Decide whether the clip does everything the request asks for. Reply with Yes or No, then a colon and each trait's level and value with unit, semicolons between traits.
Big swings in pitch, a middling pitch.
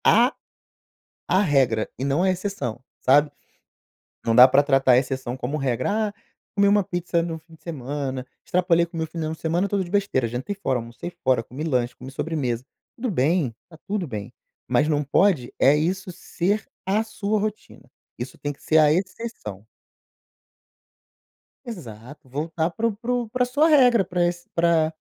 Yes: wide, 6.7 semitones; medium, 160 Hz